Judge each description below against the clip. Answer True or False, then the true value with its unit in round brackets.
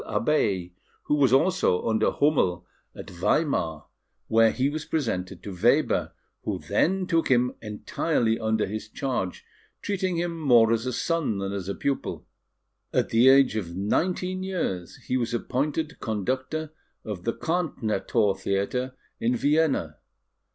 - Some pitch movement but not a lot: False (7.0 semitones)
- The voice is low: True (120 Hz)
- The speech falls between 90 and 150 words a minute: True (140 wpm)